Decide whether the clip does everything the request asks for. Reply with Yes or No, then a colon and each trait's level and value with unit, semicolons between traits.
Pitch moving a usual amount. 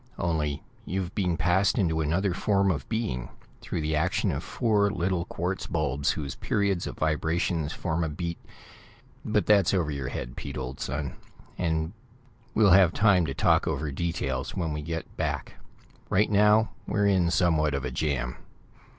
Yes: average, 4.3 semitones